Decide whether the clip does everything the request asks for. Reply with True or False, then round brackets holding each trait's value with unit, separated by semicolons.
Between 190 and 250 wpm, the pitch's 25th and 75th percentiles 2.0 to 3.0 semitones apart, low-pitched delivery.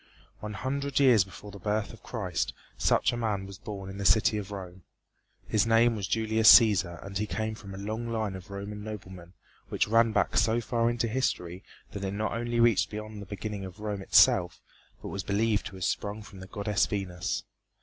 True (205 wpm; 2.5 semitones; 105 Hz)